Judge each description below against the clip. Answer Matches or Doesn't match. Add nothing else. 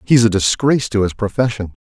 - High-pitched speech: Doesn't match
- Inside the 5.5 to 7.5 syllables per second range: Matches